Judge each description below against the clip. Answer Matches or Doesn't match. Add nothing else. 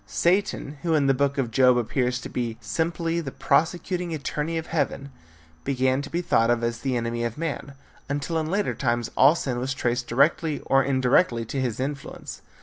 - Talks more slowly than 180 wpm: Doesn't match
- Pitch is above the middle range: Doesn't match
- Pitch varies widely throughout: Doesn't match